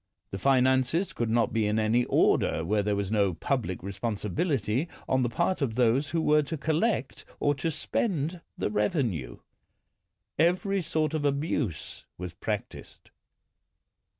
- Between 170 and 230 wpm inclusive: No, average, 150 wpm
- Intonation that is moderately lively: No, wide, 6.8 semitones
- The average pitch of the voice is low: Yes, low, 130 Hz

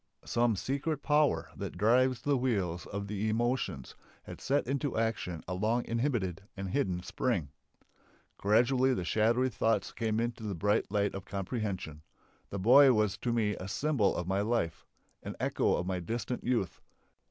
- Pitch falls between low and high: No, low, 110 Hz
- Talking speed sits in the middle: Yes, average, 165 wpm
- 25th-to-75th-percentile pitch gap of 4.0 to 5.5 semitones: Yes, average, 4.4 semitones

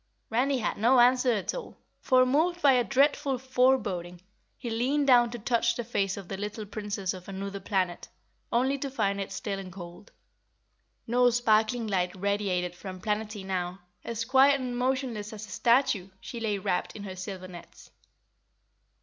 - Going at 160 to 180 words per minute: Yes, average, 170 wpm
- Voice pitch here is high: Yes, high, 220 Hz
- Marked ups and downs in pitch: No, average, 4.5 semitones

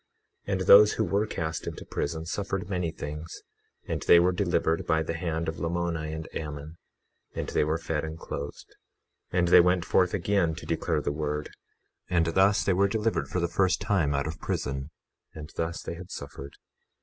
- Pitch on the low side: Yes, very low, 85 Hz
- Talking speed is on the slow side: No, average, 195 wpm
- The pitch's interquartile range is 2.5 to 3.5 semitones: Yes, average, 2.8 semitones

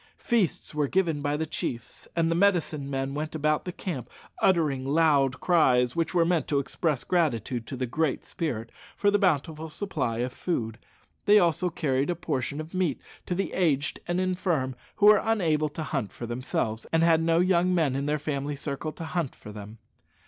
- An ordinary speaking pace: Yes, average, 190 wpm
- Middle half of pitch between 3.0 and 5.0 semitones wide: Yes, average, 4.4 semitones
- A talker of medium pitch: Yes, medium, 155 Hz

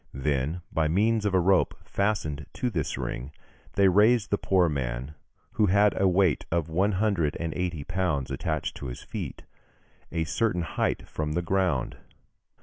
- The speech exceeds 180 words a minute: No, average, 165 wpm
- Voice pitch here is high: No, very low, 90 Hz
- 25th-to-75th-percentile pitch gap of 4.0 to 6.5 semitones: Yes, average, 4.6 semitones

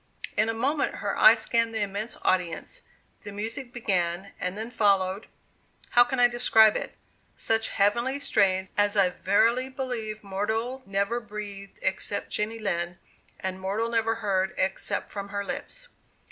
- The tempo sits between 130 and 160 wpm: Yes, average, 150 wpm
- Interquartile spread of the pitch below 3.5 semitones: Yes, average, 3.0 semitones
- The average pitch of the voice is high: Yes, high, 210 Hz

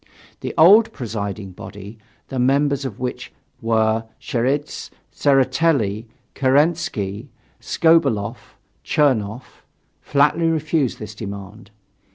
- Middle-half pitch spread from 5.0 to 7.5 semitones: Yes, average, 5.3 semitones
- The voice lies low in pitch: Yes, low, 125 Hz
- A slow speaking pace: Yes, slow, 90 wpm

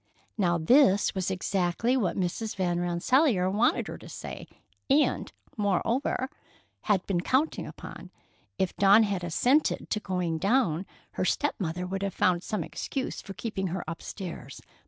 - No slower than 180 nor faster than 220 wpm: No, average, 150 wpm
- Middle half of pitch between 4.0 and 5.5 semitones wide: Yes, average, 4.3 semitones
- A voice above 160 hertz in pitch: Yes, high, 190 Hz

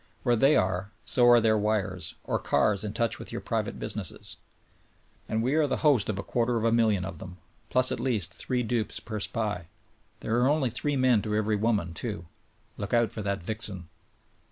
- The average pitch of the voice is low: Yes, low, 110 Hz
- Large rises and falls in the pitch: No, average, 3.2 semitones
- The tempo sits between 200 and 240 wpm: Yes, fast, 205 wpm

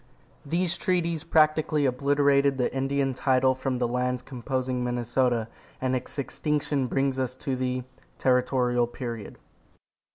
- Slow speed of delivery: Yes, slow, 125 wpm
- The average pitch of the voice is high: No, low, 130 Hz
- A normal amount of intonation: No, narrow, 2.0 semitones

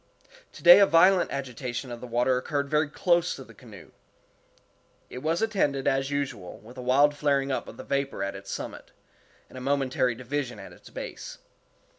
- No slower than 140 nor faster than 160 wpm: No, average, 180 wpm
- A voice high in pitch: No, low, 135 Hz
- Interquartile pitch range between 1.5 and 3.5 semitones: Yes, average, 2.8 semitones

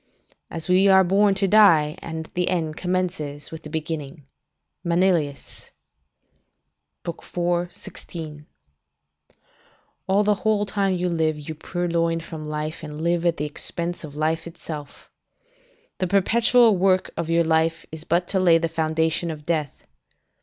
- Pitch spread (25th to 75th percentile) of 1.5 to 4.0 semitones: Yes, average, 2.7 semitones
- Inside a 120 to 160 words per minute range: Yes, average, 145 wpm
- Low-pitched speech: No, medium, 170 Hz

